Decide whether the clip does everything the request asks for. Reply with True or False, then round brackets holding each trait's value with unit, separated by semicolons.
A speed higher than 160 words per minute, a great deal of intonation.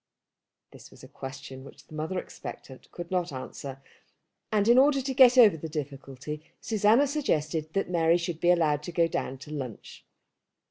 True (175 wpm; 6.1 semitones)